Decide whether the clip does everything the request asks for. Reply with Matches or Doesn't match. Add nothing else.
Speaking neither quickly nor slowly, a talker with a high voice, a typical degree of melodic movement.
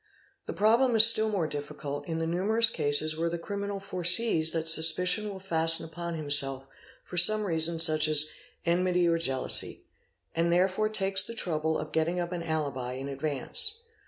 Doesn't match